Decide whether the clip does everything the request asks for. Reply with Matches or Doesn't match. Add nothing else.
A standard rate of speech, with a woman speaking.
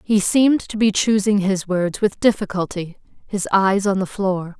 Matches